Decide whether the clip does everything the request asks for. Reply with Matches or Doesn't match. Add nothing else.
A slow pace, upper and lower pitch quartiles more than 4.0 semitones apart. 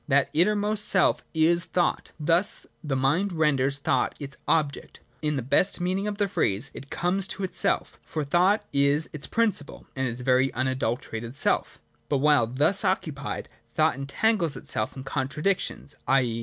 Doesn't match